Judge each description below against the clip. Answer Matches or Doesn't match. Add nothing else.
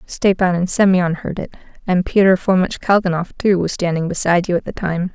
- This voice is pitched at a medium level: Matches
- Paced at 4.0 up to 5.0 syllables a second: Doesn't match